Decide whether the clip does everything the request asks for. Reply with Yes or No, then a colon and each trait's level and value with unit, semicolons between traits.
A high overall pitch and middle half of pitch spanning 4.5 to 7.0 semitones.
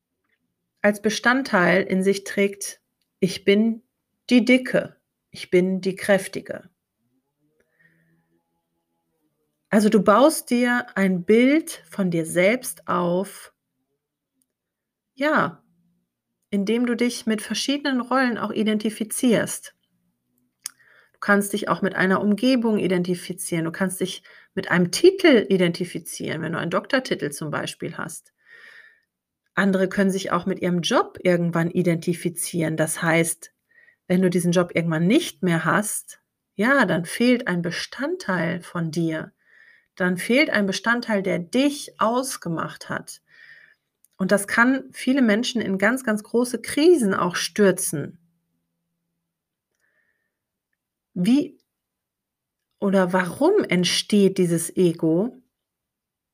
Yes: high, 195 Hz; wide, 5.6 semitones